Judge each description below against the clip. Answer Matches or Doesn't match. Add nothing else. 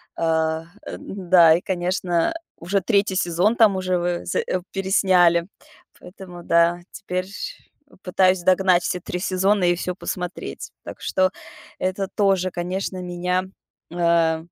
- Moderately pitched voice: Matches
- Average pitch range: Doesn't match